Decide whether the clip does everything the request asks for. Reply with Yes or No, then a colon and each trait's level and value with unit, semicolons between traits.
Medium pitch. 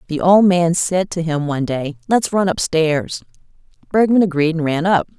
Yes: medium, 170 Hz